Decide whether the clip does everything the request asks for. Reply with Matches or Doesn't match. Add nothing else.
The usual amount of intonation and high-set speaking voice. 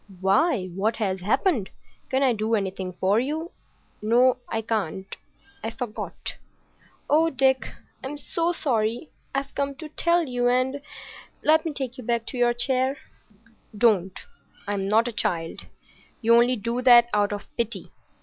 Matches